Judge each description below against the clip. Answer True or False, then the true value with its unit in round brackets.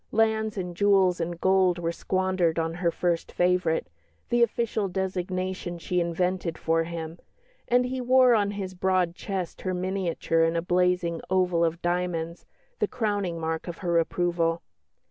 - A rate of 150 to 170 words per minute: True (155 wpm)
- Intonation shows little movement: True (2.1 semitones)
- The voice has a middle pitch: True (180 Hz)